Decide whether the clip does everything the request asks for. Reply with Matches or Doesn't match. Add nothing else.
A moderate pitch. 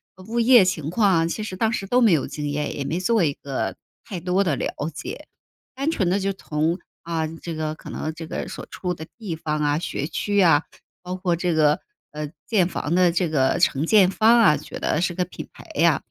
Matches